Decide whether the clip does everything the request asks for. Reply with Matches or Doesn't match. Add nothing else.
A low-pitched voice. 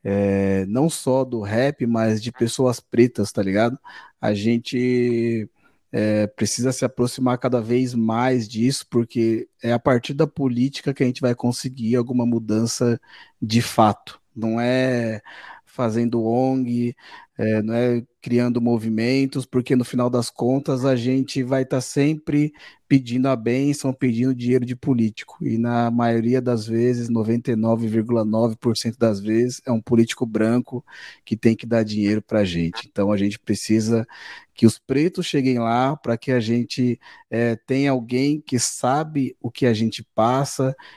Matches